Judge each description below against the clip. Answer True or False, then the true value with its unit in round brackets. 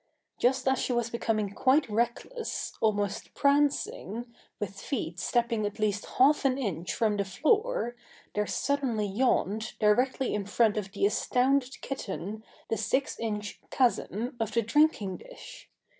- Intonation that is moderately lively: True (4.2 semitones)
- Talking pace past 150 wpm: False (145 wpm)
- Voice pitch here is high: True (230 Hz)